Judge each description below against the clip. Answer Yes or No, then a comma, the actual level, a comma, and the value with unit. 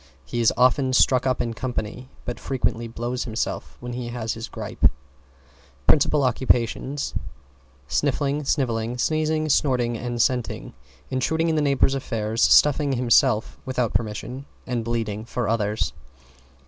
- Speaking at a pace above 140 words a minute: No, slow, 135 wpm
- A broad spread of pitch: No, average, 2.8 semitones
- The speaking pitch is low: Yes, low, 125 Hz